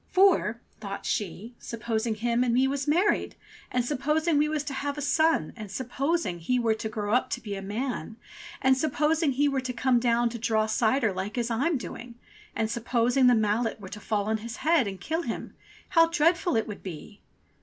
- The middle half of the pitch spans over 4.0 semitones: Yes, average, 4.7 semitones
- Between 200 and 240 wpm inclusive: Yes, fast, 205 wpm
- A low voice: No, high, 240 Hz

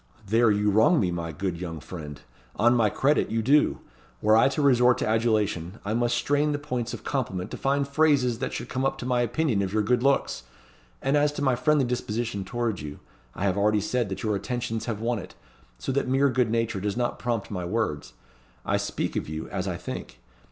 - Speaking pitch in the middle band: No, low, 115 Hz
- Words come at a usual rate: No, fast, 220 wpm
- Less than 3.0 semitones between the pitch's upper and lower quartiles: No, average, 4.2 semitones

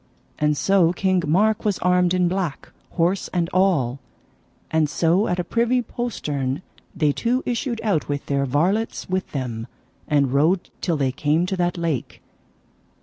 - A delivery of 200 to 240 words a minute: No, average, 155 wpm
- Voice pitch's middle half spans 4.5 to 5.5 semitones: Yes, average, 4.8 semitones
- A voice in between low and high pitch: Yes, medium, 175 Hz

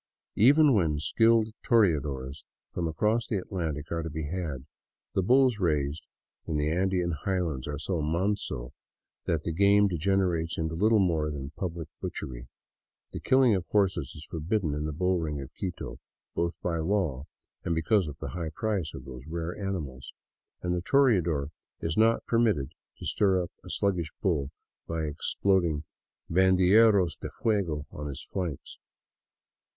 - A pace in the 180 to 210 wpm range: No, average, 155 wpm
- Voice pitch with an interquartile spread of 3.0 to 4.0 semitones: No, average, 4.4 semitones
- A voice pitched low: Yes, very low, 85 Hz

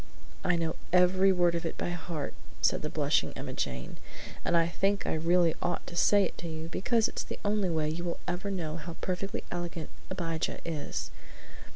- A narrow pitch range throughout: Yes, narrow, 2.0 semitones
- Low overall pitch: No, medium, 175 Hz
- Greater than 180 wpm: Yes, average, 195 wpm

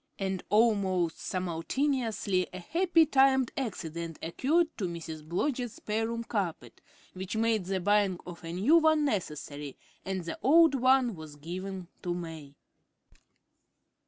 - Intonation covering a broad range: Yes, wide, 6.9 semitones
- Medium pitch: No, high, 195 Hz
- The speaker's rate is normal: No, slow, 130 wpm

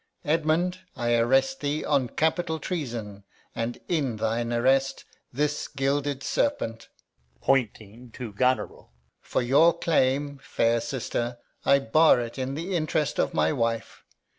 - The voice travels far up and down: No, average, 4.2 semitones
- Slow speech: Yes, slow, 130 wpm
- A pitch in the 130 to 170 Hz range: Yes, low, 135 Hz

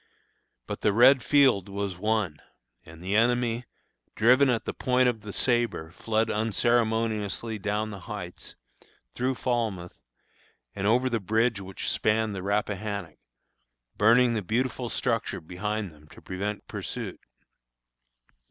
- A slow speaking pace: Yes, slow, 130 wpm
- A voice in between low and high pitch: No, low, 110 Hz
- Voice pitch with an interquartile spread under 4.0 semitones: Yes, average, 3.1 semitones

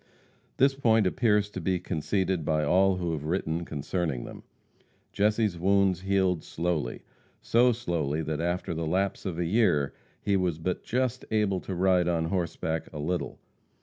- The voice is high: No, very low, 90 Hz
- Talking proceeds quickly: No, average, 160 wpm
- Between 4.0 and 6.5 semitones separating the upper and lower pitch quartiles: No, average, 3.4 semitones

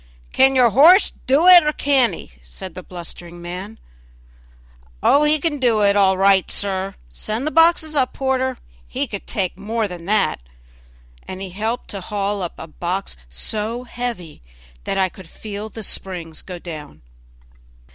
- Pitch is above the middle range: Yes, high, 200 Hz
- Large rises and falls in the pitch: Yes, wide, 5.8 semitones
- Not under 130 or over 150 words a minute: No, average, 165 wpm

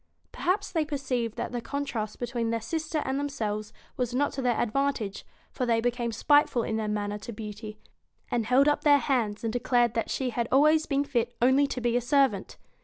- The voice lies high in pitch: Yes, high, 245 Hz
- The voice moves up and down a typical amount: Yes, average, 3.7 semitones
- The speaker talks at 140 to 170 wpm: No, fast, 205 wpm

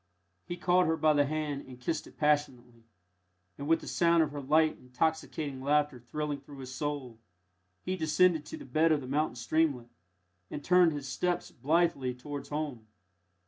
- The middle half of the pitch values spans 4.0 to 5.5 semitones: No, average, 3.2 semitones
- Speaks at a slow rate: No, average, 175 wpm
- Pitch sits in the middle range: Yes, medium, 150 Hz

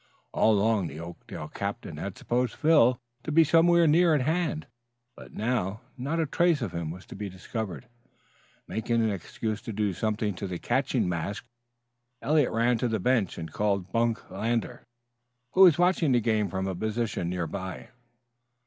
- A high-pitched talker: No, low, 110 Hz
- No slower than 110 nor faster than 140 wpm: No, average, 175 wpm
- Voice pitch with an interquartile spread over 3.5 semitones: Yes, wide, 5.4 semitones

